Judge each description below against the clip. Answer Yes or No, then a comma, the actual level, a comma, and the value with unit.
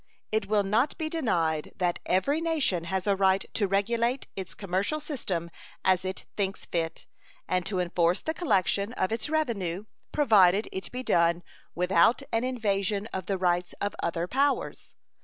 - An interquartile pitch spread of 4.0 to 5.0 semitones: Yes, average, 4.6 semitones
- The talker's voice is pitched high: Yes, high, 195 Hz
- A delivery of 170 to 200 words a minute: No, average, 160 wpm